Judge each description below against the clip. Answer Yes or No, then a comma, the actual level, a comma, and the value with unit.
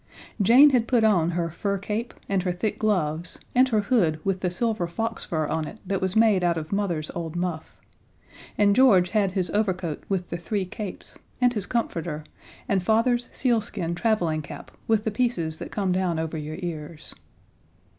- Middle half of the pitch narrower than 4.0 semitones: No, average, 4.4 semitones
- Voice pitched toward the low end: No, high, 190 Hz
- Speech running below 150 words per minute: No, average, 185 wpm